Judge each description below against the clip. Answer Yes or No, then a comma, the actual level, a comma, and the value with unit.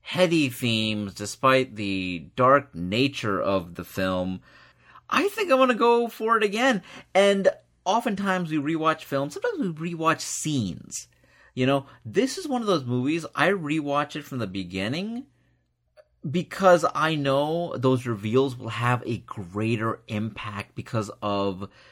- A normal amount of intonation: No, wide, 8.9 semitones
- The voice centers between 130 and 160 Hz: Yes, medium, 140 Hz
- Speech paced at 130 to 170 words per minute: Yes, average, 140 wpm